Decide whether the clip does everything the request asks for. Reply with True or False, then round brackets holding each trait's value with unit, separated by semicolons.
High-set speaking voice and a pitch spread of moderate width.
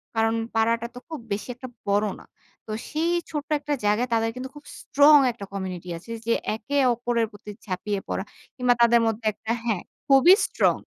True (230 Hz; 4.1 semitones)